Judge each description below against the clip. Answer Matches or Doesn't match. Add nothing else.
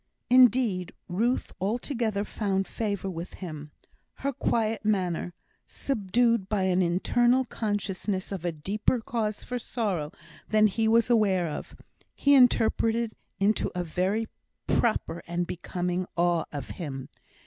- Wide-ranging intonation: Doesn't match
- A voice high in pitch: Matches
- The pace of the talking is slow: Matches